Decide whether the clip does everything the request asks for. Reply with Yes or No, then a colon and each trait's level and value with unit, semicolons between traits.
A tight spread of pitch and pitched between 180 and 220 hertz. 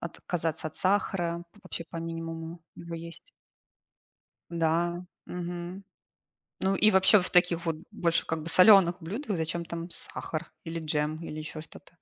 No: narrow, 1.5 semitones; medium, 170 Hz